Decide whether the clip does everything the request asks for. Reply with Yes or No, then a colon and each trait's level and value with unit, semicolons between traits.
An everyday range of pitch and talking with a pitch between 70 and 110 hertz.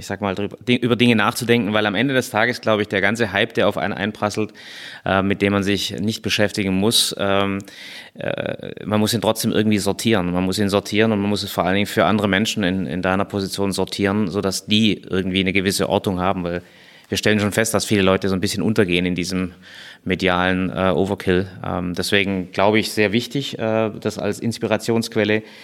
No: narrow, 2.3 semitones; low, 100 Hz